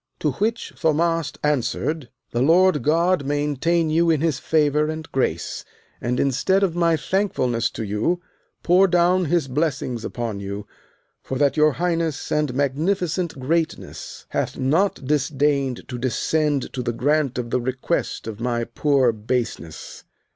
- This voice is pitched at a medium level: Yes, medium, 145 Hz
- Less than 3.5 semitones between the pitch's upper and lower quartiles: No, average, 4.7 semitones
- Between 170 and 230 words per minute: No, average, 145 wpm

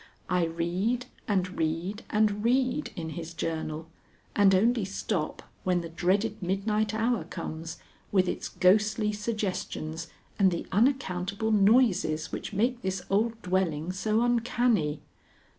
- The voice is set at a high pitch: Yes, high, 195 Hz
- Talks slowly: Yes, slow, 125 wpm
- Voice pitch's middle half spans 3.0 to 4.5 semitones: Yes, average, 4.1 semitones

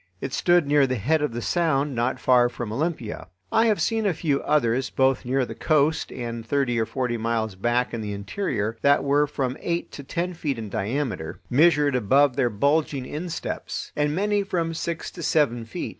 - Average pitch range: Yes, average, 4.7 semitones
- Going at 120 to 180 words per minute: No, average, 195 wpm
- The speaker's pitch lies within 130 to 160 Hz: Yes, low, 135 Hz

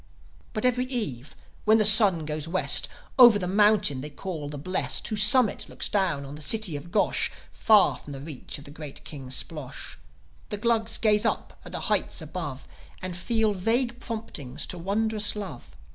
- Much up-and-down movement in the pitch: Yes, wide, 6.5 semitones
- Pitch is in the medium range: No, high, 195 Hz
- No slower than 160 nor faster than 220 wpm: Yes, average, 180 wpm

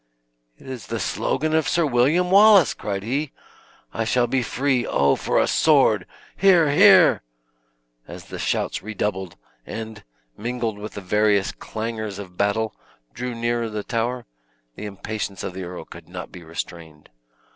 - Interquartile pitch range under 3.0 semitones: No, average, 4.7 semitones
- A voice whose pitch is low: Yes, low, 110 Hz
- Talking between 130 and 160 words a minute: Yes, average, 155 wpm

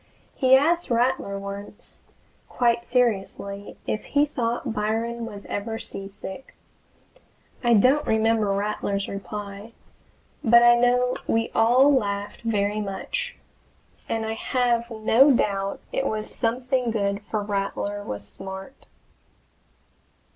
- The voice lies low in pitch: No, high, 225 Hz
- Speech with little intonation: No, average, 3.3 semitones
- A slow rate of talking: Yes, slow, 115 wpm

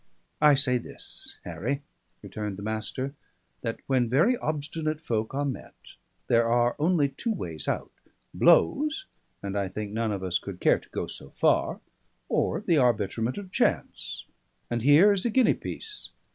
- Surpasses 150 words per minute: Yes, average, 160 wpm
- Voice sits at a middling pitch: No, low, 130 Hz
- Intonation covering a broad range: Yes, wide, 6.5 semitones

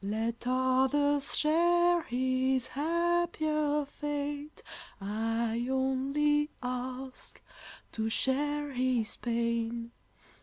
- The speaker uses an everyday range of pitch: Yes, average, 3.7 semitones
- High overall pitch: Yes, very high, 265 Hz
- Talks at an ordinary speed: No, slow, 75 wpm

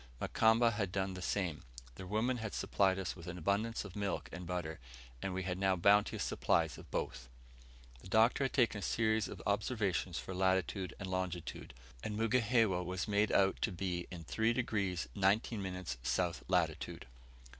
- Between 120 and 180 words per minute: Yes, average, 175 wpm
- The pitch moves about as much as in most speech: Yes, average, 3.0 semitones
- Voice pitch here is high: No, very low, 95 Hz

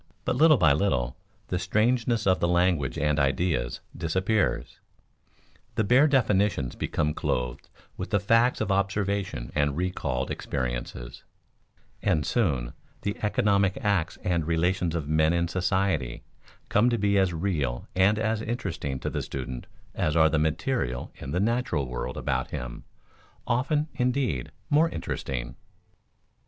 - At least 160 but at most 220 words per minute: No, average, 140 wpm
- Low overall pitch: Yes, very low, 90 Hz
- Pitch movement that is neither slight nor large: No, wide, 6.5 semitones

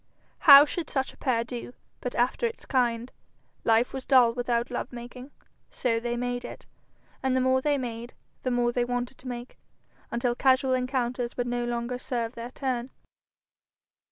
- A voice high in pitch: Yes, high, 245 Hz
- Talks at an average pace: Yes, average, 170 wpm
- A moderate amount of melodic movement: No, narrow, 1.4 semitones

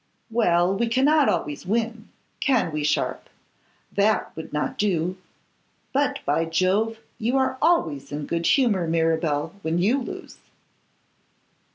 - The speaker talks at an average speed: No, slow, 130 wpm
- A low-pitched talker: No, high, 190 Hz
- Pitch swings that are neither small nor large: No, wide, 6.4 semitones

